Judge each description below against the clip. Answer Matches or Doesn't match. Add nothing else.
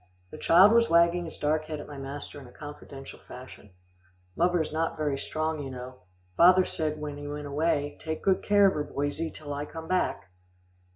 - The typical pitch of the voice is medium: Matches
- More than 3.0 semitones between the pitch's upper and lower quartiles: Doesn't match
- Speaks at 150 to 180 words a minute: Doesn't match